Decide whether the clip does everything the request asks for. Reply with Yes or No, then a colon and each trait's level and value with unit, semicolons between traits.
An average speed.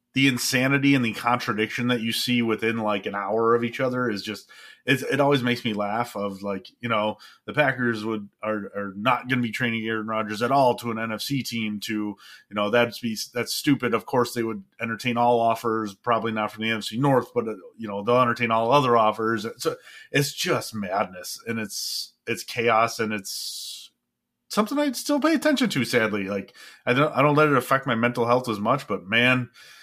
No: fast, 215 wpm